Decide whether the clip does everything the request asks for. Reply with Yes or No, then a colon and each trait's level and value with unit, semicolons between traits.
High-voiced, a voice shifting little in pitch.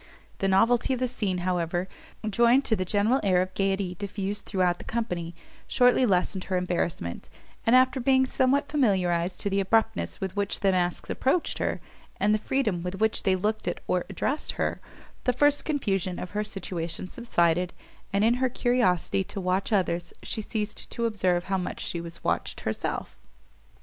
No: high, 195 Hz; average, 4.5 semitones